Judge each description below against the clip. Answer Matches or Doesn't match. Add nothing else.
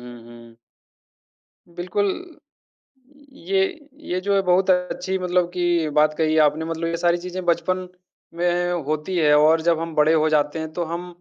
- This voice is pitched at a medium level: Matches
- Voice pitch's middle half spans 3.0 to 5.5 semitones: Doesn't match